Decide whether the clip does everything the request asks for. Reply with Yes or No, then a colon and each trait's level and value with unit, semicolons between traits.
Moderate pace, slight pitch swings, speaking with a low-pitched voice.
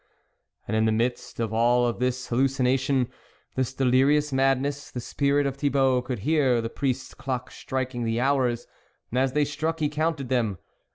Yes: average, 170 wpm; narrow, 2.3 semitones; low, 130 Hz